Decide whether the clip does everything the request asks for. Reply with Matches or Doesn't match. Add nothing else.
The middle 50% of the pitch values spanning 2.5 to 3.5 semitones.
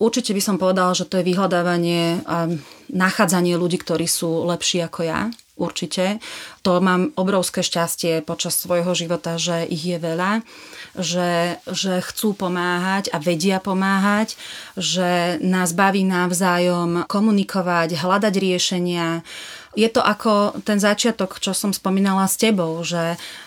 Doesn't match